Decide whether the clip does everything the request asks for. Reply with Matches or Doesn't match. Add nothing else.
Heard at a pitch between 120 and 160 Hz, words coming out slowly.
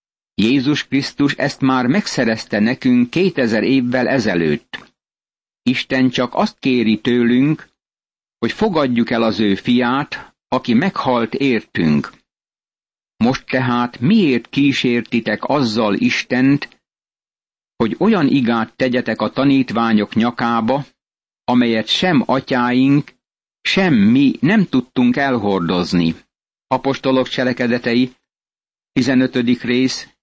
Matches